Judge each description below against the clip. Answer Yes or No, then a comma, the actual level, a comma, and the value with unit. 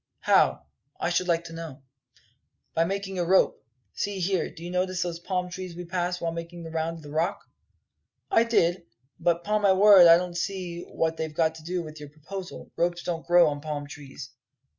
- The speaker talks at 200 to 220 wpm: Yes, fast, 205 wpm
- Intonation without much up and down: Yes, narrow, 2.0 semitones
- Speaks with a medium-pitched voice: Yes, medium, 175 Hz